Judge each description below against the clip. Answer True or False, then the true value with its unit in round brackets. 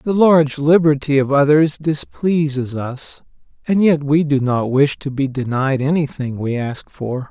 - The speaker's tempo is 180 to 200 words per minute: False (165 wpm)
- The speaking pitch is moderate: True (145 Hz)